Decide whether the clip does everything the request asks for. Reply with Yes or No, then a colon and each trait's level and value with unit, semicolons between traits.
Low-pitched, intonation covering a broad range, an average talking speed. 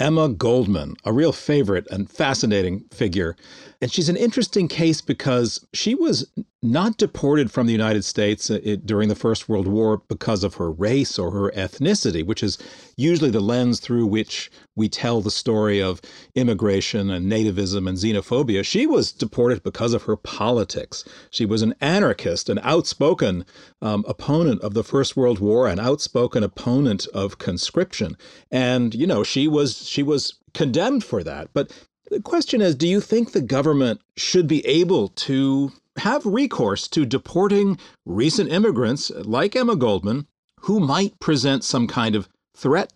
Yes: low, 120 Hz; wide, 7.0 semitones; average, 160 wpm